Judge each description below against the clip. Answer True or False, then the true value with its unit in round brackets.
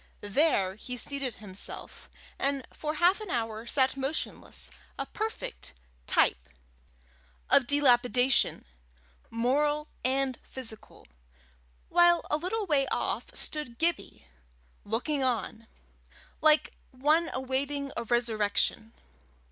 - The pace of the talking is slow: True (100 wpm)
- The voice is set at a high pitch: True (265 Hz)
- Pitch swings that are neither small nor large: True (4.5 semitones)